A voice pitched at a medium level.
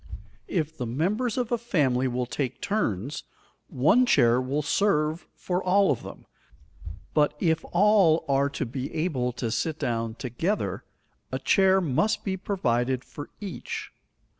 Yes: medium, 150 Hz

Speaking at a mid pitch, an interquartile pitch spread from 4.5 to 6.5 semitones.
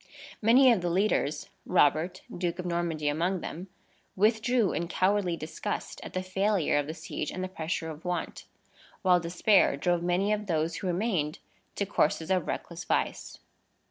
No: medium, 180 Hz; average, 2.8 semitones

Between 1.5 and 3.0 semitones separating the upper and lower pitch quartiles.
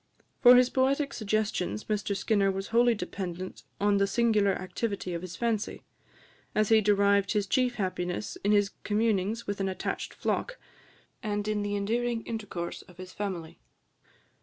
Yes: narrow, 2.6 semitones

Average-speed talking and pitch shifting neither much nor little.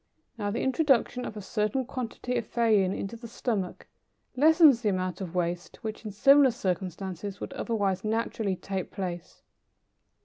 Yes: average, 150 wpm; average, 4.1 semitones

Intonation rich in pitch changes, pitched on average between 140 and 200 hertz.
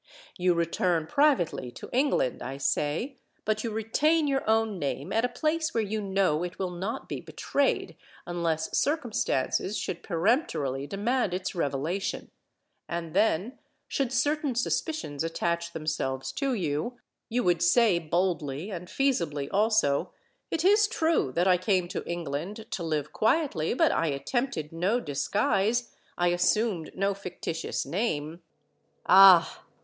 Yes: wide, 6.4 semitones; medium, 185 Hz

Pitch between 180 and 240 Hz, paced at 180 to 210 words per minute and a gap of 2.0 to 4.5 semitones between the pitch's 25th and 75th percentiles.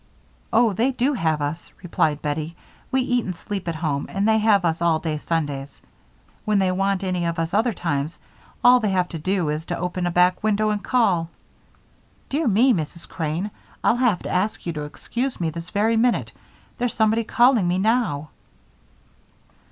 No: medium, 185 Hz; average, 185 wpm; average, 5.1 semitones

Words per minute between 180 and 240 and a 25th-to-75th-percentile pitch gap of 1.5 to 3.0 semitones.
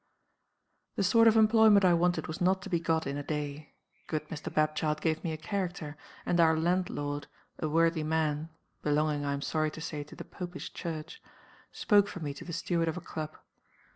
Yes: average, 200 wpm; average, 2.7 semitones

